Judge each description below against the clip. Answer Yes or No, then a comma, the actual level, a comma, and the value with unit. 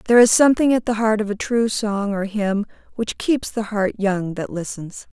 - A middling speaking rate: No, fast, 220 wpm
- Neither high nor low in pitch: No, high, 215 Hz